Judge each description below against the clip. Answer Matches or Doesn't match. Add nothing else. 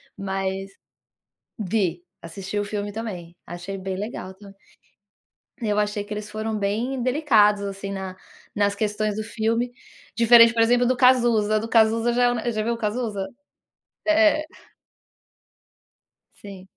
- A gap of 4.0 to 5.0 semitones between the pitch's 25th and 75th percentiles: Doesn't match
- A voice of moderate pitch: Doesn't match